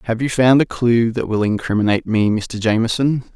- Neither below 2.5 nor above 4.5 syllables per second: No, 5.5 syllables/s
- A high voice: No, low, 115 Hz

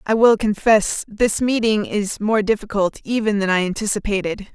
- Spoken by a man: No, female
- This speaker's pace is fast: No, average, 160 wpm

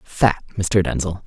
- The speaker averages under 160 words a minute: Yes, average, 140 wpm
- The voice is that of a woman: No, male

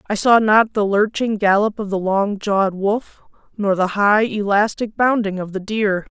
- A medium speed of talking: Yes, average, 185 wpm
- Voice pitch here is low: No, high, 205 Hz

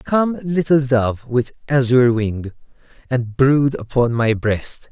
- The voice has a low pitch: Yes, low, 130 Hz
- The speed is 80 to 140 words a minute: Yes, slow, 135 wpm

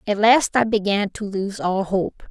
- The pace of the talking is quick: Yes, fast, 210 wpm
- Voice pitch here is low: No, high, 205 Hz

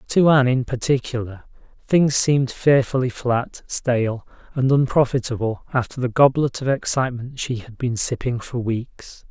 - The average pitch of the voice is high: No, low, 125 Hz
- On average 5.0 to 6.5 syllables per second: No, 4.8 syllables/s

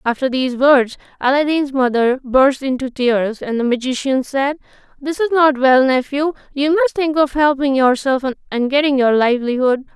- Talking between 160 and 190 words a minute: Yes, average, 165 wpm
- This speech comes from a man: No, female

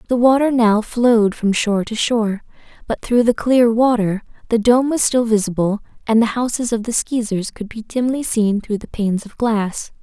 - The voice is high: Yes, high, 225 Hz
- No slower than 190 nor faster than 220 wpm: Yes, average, 200 wpm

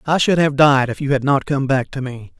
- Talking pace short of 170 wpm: No, fast, 300 wpm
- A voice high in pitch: No, medium, 140 Hz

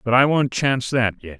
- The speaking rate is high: Yes, fast, 260 wpm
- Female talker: No, male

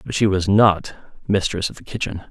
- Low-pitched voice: Yes, very low, 95 Hz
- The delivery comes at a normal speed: No, fast, 210 wpm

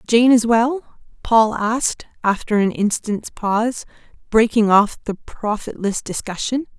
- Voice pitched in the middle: No, high, 220 Hz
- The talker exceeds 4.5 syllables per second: No, 4.1 syllables/s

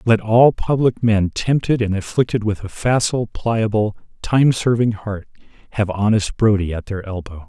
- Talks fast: No, average, 160 wpm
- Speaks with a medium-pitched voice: No, low, 110 Hz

